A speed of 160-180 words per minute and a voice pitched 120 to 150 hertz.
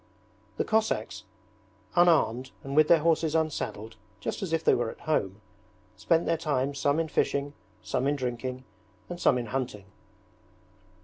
No: average, 150 wpm; medium, 140 Hz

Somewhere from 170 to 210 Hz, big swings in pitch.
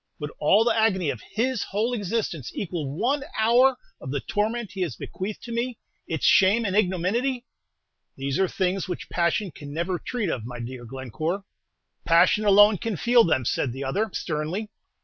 Yes: high, 190 Hz; wide, 6.5 semitones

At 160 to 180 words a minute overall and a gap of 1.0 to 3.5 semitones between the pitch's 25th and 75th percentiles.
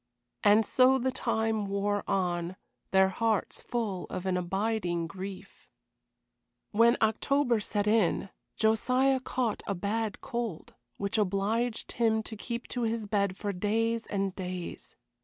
No: slow, 135 wpm; average, 2.8 semitones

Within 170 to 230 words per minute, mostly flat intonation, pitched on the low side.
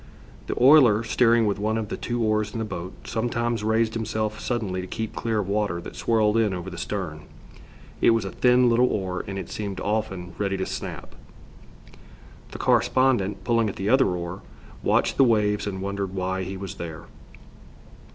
No: average, 185 wpm; average, 3.0 semitones; low, 105 Hz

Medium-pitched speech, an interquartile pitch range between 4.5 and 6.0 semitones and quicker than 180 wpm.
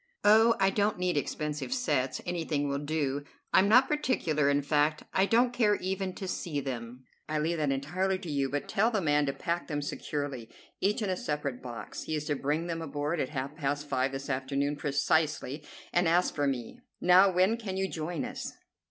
Yes: medium, 155 Hz; average, 4.9 semitones; average, 200 wpm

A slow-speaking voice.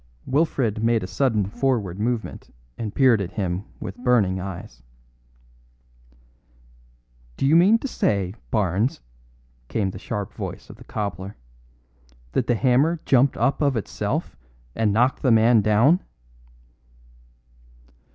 Yes: slow, 125 wpm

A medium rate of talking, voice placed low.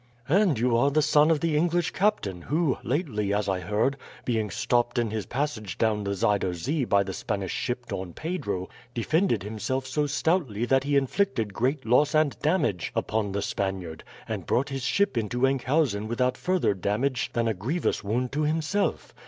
Yes: average, 180 wpm; low, 125 Hz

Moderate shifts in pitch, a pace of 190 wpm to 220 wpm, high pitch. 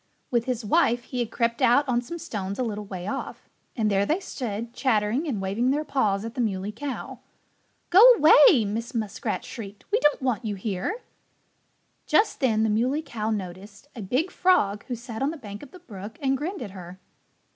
Yes: average, 4.7 semitones; average, 200 wpm; high, 230 Hz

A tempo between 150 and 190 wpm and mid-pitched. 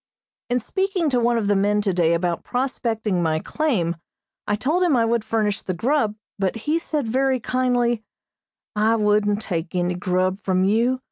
No: average, 175 wpm; high, 220 Hz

